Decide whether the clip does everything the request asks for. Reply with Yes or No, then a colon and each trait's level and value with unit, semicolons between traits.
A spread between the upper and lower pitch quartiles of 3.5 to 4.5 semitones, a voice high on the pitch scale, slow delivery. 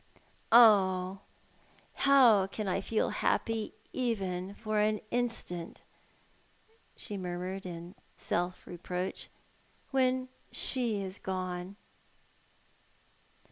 Yes: average, 3.8 semitones; high, 195 Hz; slow, 85 wpm